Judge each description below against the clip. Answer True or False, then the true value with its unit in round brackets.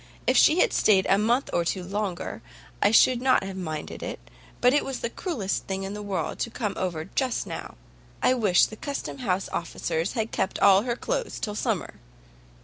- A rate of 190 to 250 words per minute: True (200 wpm)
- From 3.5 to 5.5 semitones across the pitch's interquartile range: True (4.5 semitones)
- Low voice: False (205 Hz)